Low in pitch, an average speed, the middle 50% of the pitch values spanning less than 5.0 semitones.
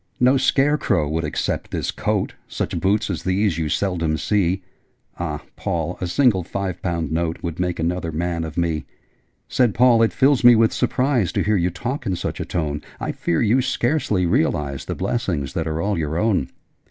No: very low, 90 Hz; average, 190 wpm; wide, 5.5 semitones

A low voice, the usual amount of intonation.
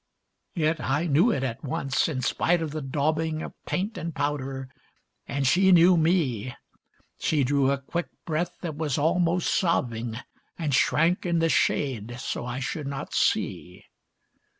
No: medium, 150 Hz; average, 3.9 semitones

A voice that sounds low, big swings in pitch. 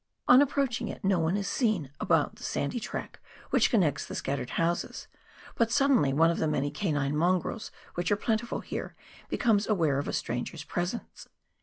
No: medium, 180 Hz; wide, 7.3 semitones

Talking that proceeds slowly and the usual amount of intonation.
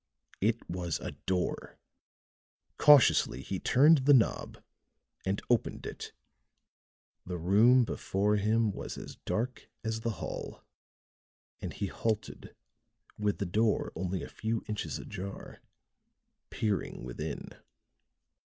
Yes: slow, 115 wpm; average, 3.5 semitones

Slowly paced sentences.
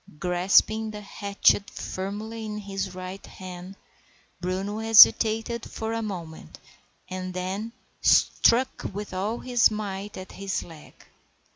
Yes: slow, 120 wpm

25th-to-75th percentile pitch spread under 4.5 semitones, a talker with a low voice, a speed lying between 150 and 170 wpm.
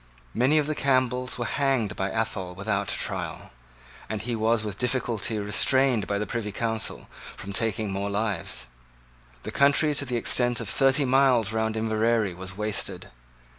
Yes: average, 3.6 semitones; low, 110 Hz; average, 165 wpm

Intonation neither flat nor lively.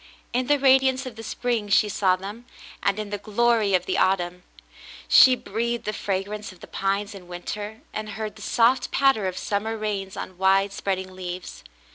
Yes: average, 3.0 semitones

